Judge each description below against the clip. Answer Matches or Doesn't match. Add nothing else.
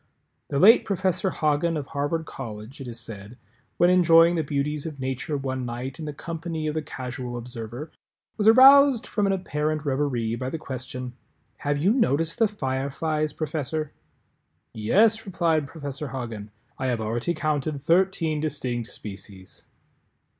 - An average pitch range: Matches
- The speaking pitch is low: Doesn't match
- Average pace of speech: Matches